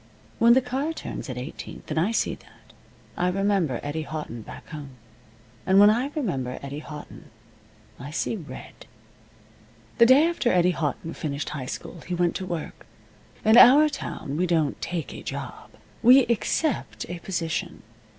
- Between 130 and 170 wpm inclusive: Yes, average, 160 wpm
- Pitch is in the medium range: Yes, medium, 175 Hz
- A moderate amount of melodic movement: No, wide, 7.4 semitones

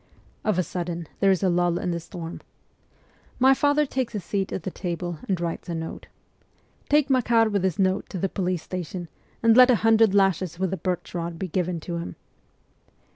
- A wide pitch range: No, average, 3.7 semitones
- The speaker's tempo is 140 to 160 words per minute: No, fast, 205 wpm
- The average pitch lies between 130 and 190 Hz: Yes, medium, 185 Hz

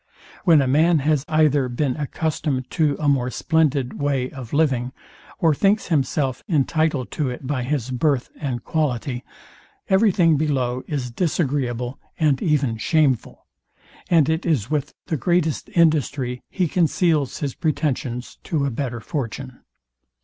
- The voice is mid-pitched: Yes, medium, 145 Hz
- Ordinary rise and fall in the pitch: Yes, average, 3.6 semitones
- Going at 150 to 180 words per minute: No, average, 140 wpm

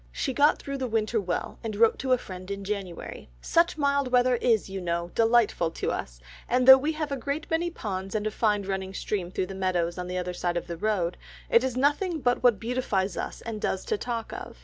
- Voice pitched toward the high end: Yes, high, 220 Hz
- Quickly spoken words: Yes, fast, 235 wpm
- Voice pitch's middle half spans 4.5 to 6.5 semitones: Yes, wide, 5.4 semitones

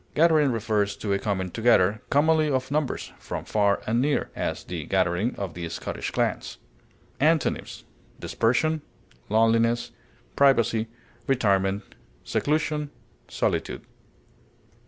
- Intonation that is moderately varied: No, wide, 6.0 semitones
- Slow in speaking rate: Yes, slow, 110 wpm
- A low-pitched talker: Yes, low, 115 Hz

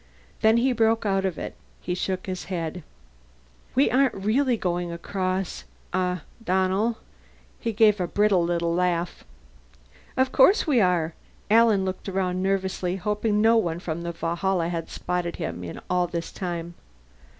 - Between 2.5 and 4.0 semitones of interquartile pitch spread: Yes, average, 3.5 semitones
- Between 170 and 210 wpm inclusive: No, average, 150 wpm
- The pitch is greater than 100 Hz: Yes, medium, 185 Hz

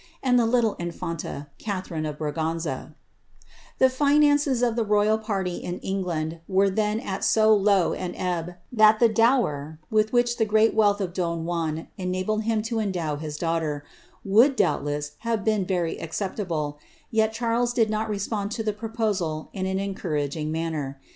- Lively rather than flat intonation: No, average, 5.0 semitones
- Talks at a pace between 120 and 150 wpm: Yes, average, 145 wpm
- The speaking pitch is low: No, high, 195 Hz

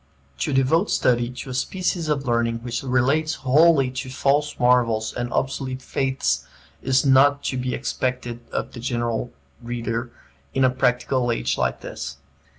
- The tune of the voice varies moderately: No, narrow, 2.2 semitones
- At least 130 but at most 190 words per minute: Yes, average, 155 wpm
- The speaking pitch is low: Yes, low, 130 Hz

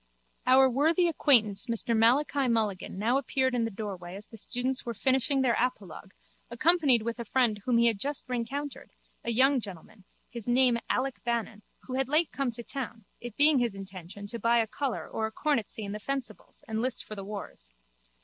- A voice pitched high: Yes, high, 235 Hz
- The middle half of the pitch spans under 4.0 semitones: Yes, average, 3.6 semitones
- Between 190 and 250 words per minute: Yes, average, 195 wpm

